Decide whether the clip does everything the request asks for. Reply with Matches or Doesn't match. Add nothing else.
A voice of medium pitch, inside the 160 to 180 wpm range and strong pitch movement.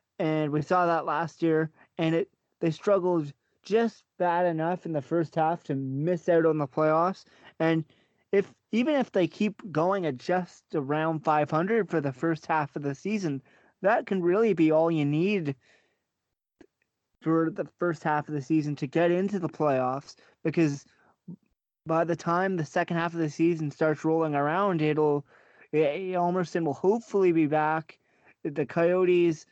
Doesn't match